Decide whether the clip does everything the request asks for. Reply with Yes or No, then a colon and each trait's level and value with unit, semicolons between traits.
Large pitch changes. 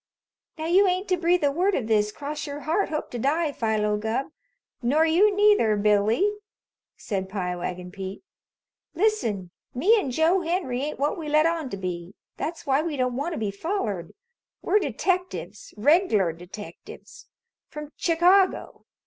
Yes: wide, 8.8 semitones